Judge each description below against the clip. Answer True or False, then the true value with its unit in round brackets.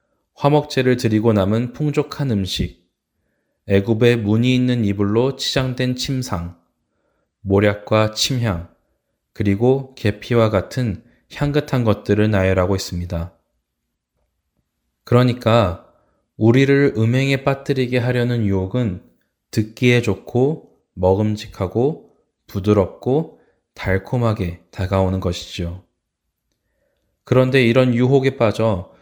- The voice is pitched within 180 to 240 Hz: False (110 Hz)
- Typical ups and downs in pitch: True (4.8 semitones)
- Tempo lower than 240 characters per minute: True (230 characters per minute)